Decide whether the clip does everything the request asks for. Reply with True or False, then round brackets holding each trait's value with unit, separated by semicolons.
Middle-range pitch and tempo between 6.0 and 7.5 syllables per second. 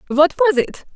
False (325 Hz; 7.0 syllables/s)